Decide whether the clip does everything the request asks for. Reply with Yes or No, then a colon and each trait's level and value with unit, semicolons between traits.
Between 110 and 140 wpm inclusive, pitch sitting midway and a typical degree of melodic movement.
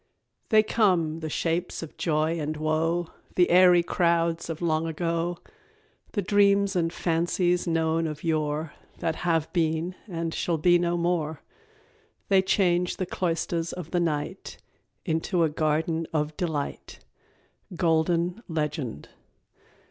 No: slow, 135 wpm; medium, 165 Hz; narrow, 1.8 semitones